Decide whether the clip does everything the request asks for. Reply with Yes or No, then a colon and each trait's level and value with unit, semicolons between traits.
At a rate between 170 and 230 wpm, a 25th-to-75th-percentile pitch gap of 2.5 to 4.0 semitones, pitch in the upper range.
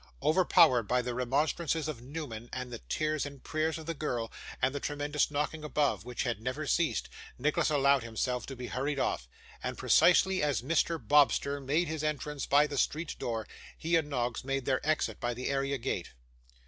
No: average, 185 wpm; average, 3.5 semitones; medium, 140 Hz